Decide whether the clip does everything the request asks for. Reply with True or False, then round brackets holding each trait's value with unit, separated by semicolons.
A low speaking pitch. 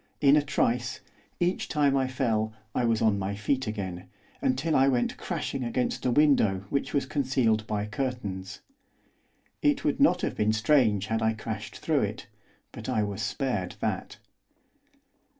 True (120 Hz)